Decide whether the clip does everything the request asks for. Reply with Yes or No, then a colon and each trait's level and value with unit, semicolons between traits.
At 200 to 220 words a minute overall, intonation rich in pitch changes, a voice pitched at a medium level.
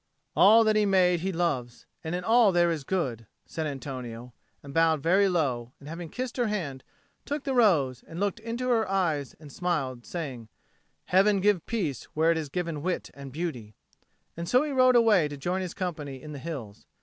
Yes: fast, 205 wpm; wide, 6.0 semitones; medium, 170 Hz